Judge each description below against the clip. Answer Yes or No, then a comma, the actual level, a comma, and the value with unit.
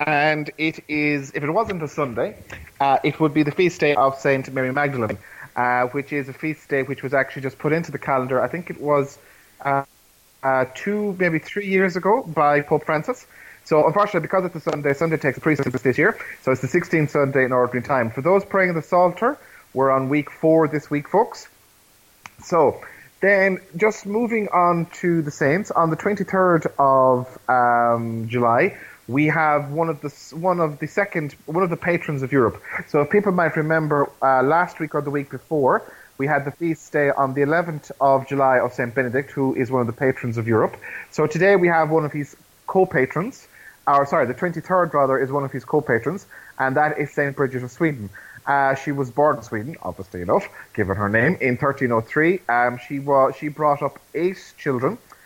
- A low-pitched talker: No, medium, 145 Hz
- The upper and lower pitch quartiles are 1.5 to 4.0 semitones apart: Yes, average, 3.7 semitones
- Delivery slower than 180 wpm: No, fast, 205 wpm